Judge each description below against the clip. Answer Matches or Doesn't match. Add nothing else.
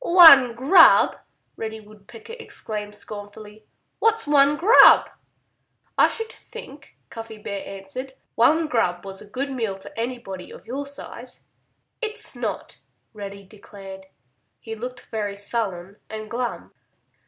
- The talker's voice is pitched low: Doesn't match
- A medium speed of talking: Doesn't match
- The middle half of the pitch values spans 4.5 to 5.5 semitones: Matches